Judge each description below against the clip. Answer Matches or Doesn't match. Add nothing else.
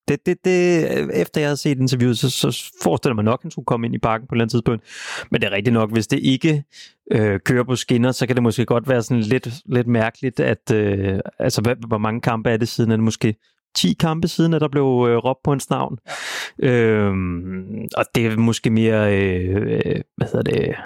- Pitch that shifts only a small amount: Doesn't match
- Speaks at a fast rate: Matches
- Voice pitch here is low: Matches